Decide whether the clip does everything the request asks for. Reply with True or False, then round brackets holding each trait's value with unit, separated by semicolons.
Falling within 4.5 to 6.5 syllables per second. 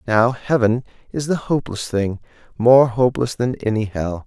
True (4.9 syllables/s)